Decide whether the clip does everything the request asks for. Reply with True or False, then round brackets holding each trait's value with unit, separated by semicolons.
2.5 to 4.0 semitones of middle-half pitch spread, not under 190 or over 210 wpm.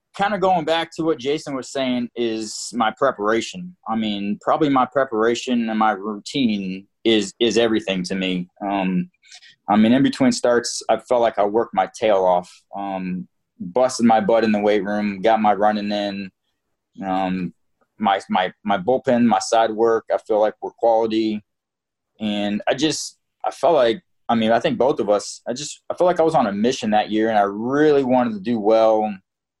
True (3.6 semitones; 195 wpm)